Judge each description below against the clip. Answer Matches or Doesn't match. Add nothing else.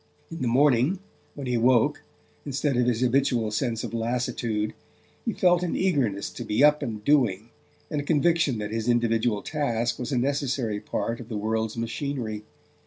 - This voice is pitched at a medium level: Doesn't match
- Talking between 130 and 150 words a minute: Doesn't match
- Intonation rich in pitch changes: Doesn't match